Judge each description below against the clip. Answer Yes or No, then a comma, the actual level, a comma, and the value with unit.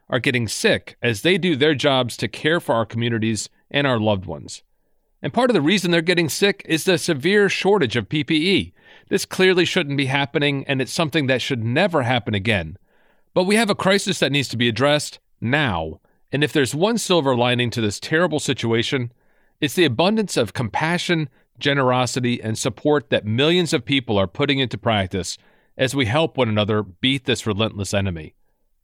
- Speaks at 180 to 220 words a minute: Yes, average, 185 wpm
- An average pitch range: No, wide, 5.9 semitones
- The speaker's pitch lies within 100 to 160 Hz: Yes, medium, 140 Hz